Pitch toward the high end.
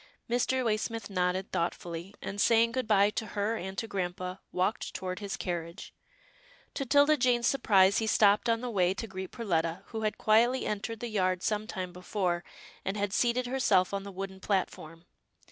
Yes: high, 200 Hz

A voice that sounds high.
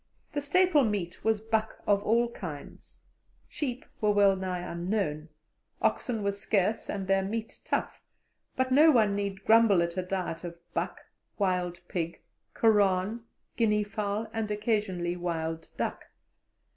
Yes: high, 205 Hz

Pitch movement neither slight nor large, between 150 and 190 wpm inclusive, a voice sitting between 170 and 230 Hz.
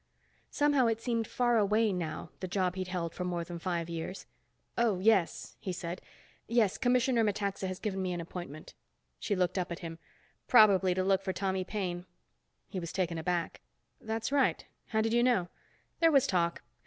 Yes: average, 3.9 semitones; average, 180 wpm; high, 190 Hz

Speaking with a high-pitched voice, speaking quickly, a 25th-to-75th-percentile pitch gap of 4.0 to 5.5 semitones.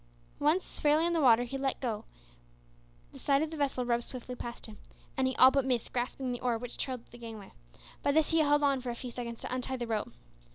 No: very high, 255 Hz; fast, 245 wpm; average, 2.8 semitones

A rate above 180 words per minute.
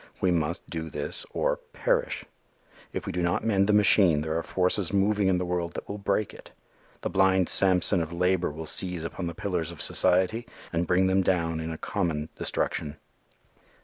Yes: average, 190 wpm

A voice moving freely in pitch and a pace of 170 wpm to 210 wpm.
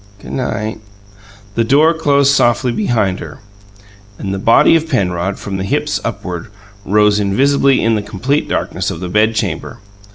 No: wide, 5.9 semitones; average, 155 wpm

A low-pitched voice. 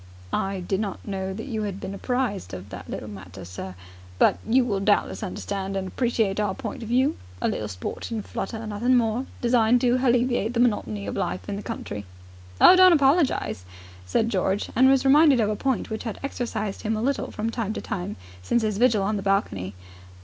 No: high, 215 Hz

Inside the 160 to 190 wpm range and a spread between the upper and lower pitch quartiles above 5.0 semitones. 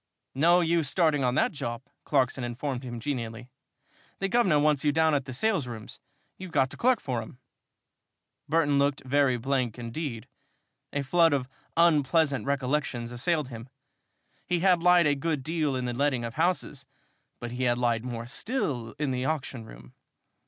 No: average, 165 wpm; average, 4.4 semitones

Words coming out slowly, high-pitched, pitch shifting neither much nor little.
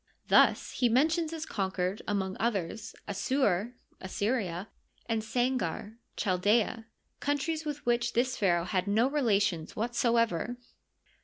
Yes: slow, 125 wpm; high, 225 Hz; average, 4.5 semitones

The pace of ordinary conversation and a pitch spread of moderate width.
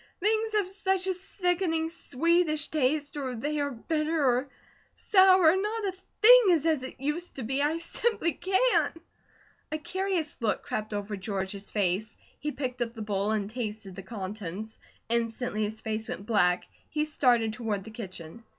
No: average, 165 wpm; wide, 7.6 semitones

